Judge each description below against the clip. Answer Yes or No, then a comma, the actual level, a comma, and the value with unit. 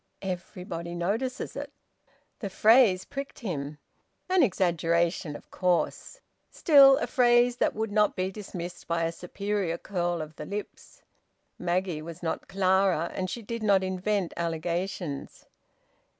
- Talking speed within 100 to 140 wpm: Yes, slow, 135 wpm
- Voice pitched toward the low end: No, medium, 185 Hz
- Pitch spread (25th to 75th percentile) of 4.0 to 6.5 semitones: No, average, 3.6 semitones